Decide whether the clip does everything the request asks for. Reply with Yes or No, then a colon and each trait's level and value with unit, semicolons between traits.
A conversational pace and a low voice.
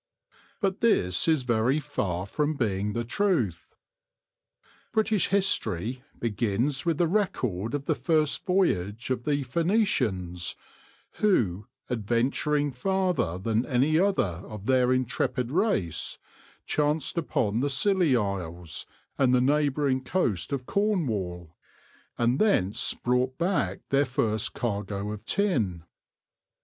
No: slow, 120 wpm; low, 125 Hz